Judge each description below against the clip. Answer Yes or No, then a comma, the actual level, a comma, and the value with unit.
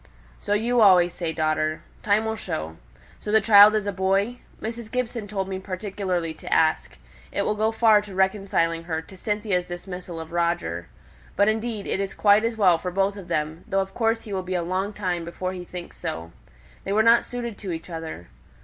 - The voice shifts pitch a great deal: No, average, 3.6 semitones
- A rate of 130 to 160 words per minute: No, fast, 205 wpm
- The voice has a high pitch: Yes, high, 195 Hz